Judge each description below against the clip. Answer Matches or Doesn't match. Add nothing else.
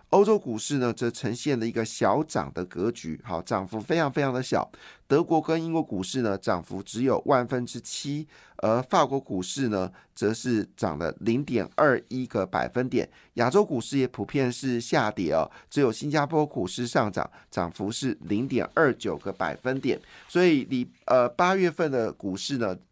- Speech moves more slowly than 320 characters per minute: Matches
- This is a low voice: Matches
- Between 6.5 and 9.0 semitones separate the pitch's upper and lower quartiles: Doesn't match